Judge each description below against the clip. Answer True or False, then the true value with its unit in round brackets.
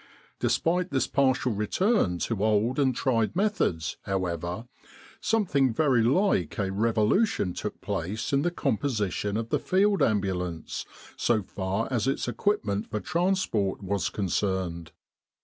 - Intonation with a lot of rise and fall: True (6.7 semitones)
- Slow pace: True (130 wpm)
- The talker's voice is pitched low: True (110 Hz)